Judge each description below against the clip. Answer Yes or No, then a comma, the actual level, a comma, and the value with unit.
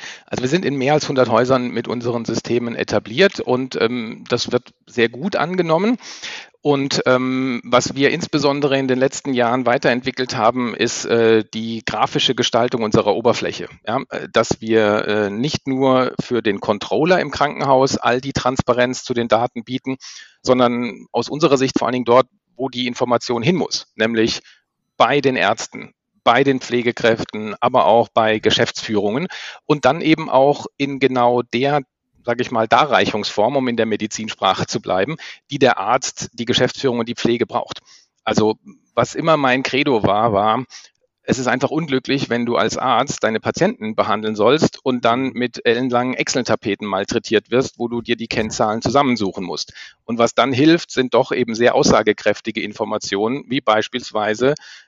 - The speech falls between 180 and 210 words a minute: No, average, 165 wpm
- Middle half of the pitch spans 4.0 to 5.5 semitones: No, average, 2.7 semitones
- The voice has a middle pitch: No, low, 125 Hz